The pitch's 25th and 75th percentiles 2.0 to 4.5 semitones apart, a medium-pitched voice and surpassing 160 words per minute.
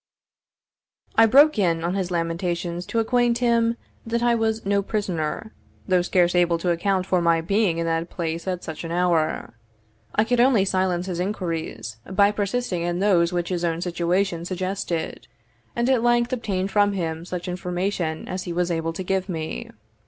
Yes: average, 3.3 semitones; medium, 180 Hz; average, 175 wpm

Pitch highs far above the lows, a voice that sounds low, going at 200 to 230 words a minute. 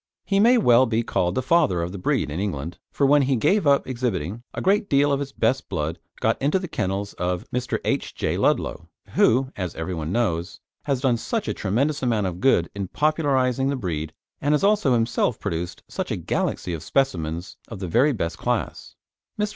Yes: wide, 7.6 semitones; low, 120 Hz; fast, 205 wpm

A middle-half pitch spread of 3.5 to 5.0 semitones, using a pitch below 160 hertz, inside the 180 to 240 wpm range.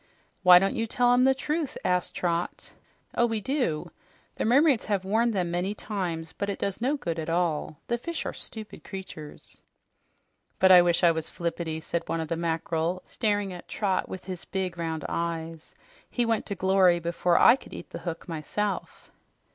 No: average, 4.3 semitones; medium, 185 Hz; average, 185 wpm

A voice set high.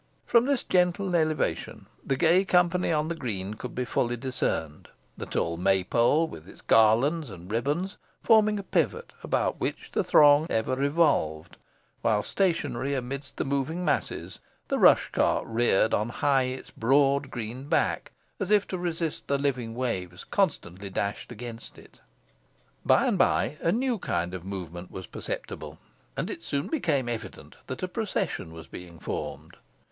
No: low, 135 Hz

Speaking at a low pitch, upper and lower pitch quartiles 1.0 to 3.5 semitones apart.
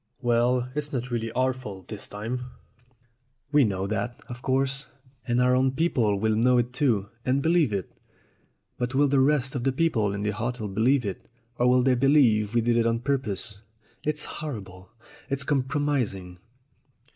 No: low, 125 Hz; average, 3.9 semitones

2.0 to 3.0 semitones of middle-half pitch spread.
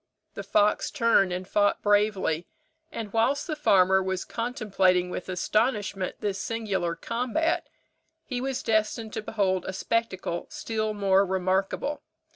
No: average, 3.4 semitones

